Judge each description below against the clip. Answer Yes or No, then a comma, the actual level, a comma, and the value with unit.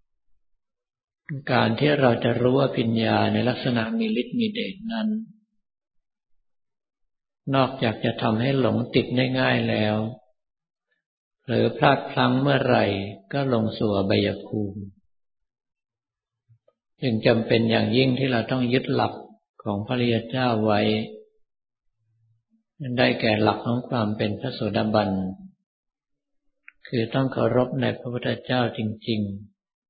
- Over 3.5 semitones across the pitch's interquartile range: No, average, 3.2 semitones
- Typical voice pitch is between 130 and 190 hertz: No, low, 120 Hz